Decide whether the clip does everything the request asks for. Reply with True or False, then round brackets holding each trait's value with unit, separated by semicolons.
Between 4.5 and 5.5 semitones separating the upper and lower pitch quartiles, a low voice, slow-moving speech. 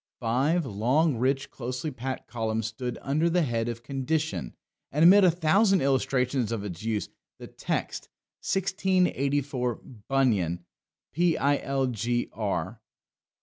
True (5.2 semitones; 130 Hz; 110 wpm)